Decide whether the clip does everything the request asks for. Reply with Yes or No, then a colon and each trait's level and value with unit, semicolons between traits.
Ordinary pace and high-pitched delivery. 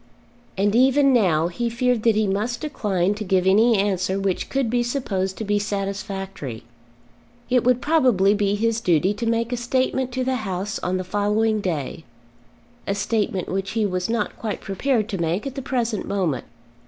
Yes: average, 180 wpm; high, 210 Hz